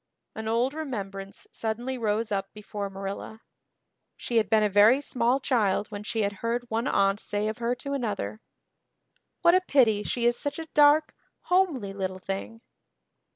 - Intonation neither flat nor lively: Yes, average, 3.9 semitones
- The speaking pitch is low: No, high, 225 Hz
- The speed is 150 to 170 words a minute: Yes, average, 165 wpm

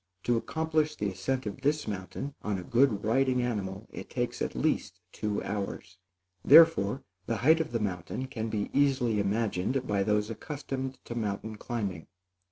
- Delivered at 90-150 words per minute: No, average, 165 wpm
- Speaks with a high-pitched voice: No, low, 115 Hz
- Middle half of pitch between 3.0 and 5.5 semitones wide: Yes, average, 4.7 semitones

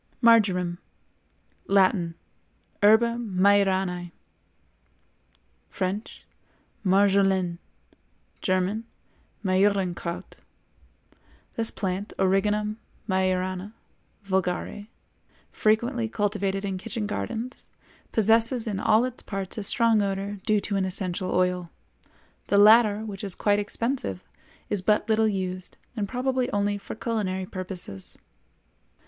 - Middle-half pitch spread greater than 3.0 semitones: No, narrow, 2.6 semitones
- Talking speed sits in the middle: No, slow, 90 wpm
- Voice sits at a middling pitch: No, high, 200 Hz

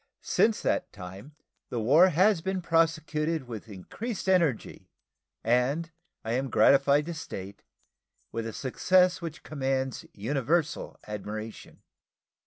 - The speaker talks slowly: Yes, slow, 115 wpm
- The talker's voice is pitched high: No, medium, 140 Hz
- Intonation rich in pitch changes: Yes, wide, 6.5 semitones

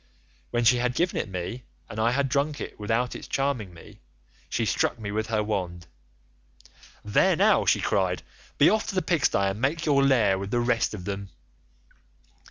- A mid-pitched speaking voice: No, low, 120 Hz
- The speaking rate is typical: Yes, average, 185 wpm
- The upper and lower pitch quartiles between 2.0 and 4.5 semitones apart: No, average, 5.3 semitones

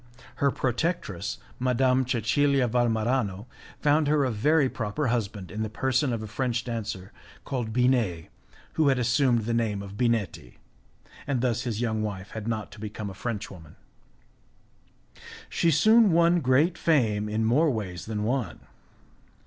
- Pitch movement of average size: Yes, average, 3.9 semitones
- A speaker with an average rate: Yes, average, 150 wpm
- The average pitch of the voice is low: Yes, low, 120 Hz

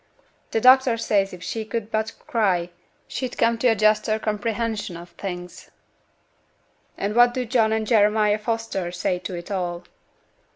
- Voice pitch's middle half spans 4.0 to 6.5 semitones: No, average, 3.0 semitones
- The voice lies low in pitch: No, high, 215 Hz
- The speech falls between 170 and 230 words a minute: No, average, 155 wpm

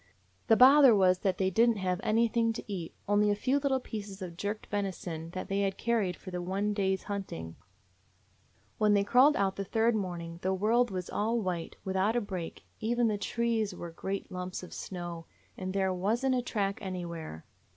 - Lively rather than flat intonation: No, average, 3.4 semitones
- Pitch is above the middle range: Yes, high, 200 Hz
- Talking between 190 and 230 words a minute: Yes, average, 195 wpm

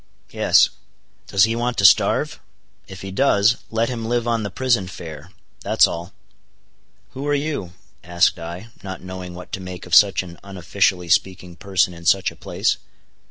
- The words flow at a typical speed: Yes, average, 170 wpm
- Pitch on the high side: No, very low, 95 Hz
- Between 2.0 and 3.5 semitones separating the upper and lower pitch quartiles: No, average, 4.1 semitones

